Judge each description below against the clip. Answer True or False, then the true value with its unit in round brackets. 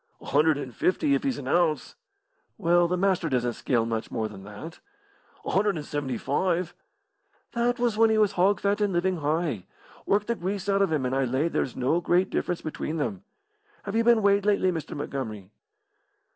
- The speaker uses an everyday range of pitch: False (6.5 semitones)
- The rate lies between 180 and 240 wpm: True (200 wpm)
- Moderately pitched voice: True (175 Hz)